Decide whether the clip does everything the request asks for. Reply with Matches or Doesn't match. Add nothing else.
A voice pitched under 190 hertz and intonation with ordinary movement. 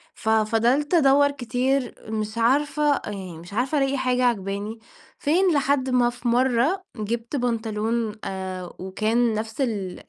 Doesn't match